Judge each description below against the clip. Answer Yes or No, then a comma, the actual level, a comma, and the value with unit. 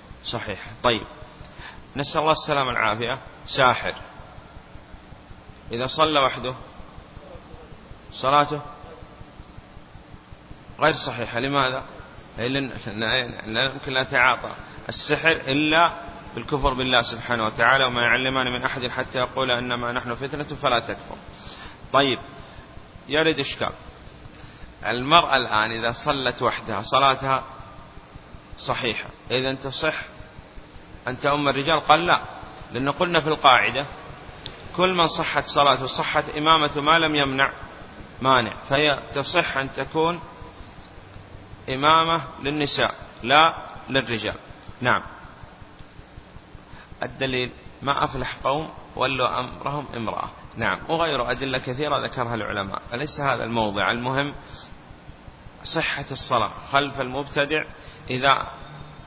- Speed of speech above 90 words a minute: Yes, average, 100 wpm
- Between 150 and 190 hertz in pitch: No, low, 135 Hz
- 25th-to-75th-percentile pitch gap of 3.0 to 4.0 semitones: Yes, average, 3.4 semitones